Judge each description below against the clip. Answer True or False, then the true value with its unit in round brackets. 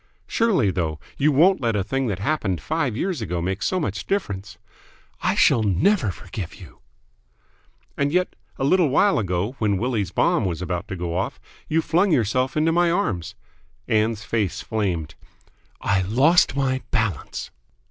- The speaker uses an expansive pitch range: True (8.3 semitones)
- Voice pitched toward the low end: True (110 Hz)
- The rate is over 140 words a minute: True (160 wpm)